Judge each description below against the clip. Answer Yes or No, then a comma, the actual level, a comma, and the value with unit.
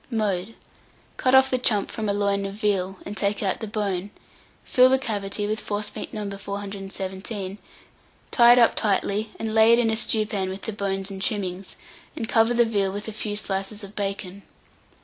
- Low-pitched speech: No, high, 205 Hz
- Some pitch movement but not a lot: No, narrow, 2.1 semitones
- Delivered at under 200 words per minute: Yes, average, 190 wpm